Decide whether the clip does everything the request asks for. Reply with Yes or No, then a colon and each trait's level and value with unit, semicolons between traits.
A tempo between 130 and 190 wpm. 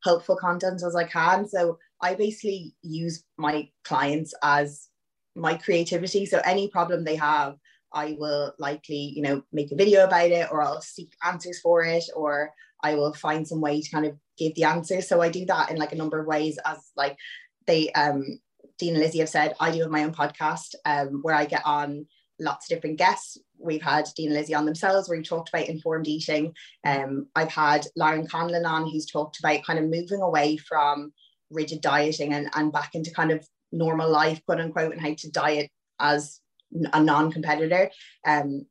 No: average, 200 wpm